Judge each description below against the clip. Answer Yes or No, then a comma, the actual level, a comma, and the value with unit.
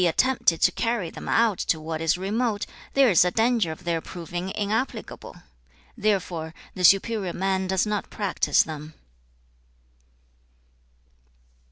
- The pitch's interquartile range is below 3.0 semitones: No, average, 4.7 semitones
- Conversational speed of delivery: No, slow, 130 wpm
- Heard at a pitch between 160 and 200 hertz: Yes, high, 190 Hz